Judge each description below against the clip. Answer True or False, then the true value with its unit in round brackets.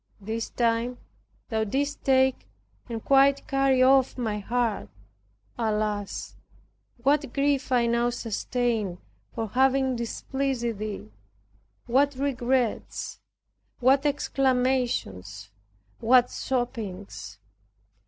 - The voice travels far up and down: False (3.1 semitones)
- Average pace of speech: False (90 wpm)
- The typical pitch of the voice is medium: False (245 Hz)